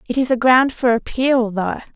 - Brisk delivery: Yes, fast, 215 wpm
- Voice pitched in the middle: No, high, 245 Hz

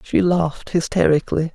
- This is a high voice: No, medium, 165 Hz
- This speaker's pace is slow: Yes, slow, 115 wpm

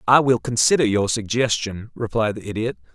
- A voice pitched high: No, low, 115 Hz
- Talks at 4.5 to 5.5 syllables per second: Yes, 5.3 syllables/s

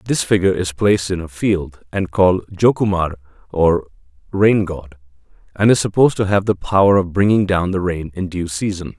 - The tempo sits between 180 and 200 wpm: Yes, average, 185 wpm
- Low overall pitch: Yes, very low, 90 Hz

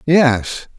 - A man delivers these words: Yes, male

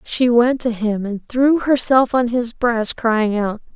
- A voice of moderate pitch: No, high, 235 Hz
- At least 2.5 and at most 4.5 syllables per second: Yes, 3.7 syllables/s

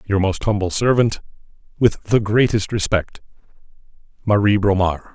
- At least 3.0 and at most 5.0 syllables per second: Yes, 4.7 syllables/s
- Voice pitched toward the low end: Yes, low, 105 Hz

